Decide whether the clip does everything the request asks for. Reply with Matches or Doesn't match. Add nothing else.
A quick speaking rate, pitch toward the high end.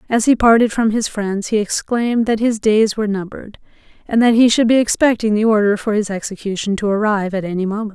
Matches